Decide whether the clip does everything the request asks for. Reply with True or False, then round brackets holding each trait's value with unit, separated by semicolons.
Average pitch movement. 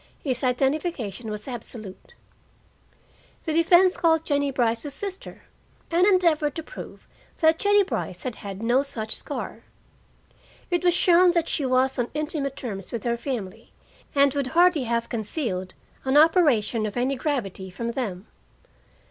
False (6.0 semitones)